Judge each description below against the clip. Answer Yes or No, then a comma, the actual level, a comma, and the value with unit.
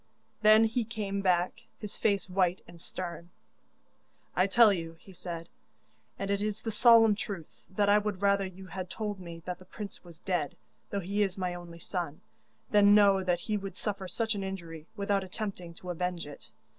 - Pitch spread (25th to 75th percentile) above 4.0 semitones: No, narrow, 2.6 semitones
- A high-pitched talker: Yes, high, 195 Hz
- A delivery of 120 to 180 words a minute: No, average, 190 wpm